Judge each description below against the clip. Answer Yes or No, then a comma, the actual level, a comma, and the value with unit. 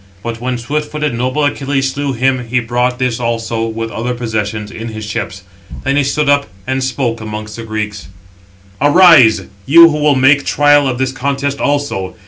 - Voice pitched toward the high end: No, low, 125 Hz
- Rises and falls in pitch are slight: No, average, 3.9 semitones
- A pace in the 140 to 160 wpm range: No, average, 180 wpm